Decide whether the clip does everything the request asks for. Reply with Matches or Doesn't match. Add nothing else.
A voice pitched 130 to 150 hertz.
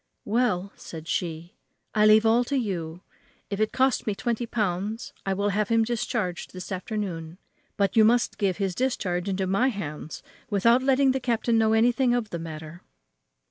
Doesn't match